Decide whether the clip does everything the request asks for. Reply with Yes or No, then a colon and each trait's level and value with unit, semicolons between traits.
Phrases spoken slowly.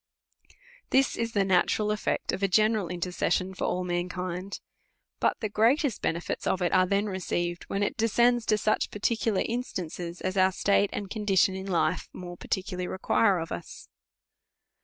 No: average, 165 wpm